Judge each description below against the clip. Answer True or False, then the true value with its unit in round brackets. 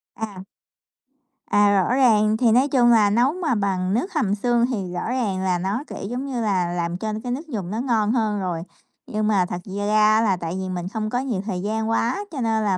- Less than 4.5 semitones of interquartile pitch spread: True (4.0 semitones)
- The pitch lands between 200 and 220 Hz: True (215 Hz)